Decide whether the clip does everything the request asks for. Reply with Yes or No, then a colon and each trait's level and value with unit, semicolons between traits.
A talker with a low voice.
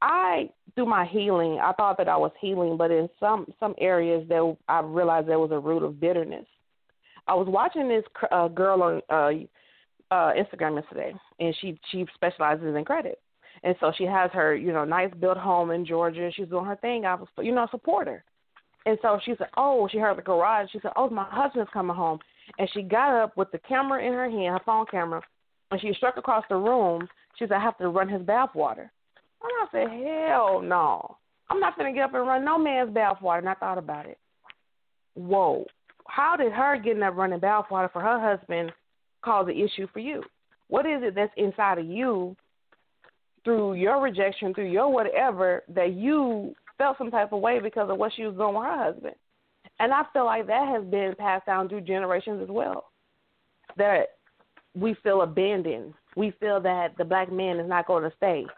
No: high, 195 Hz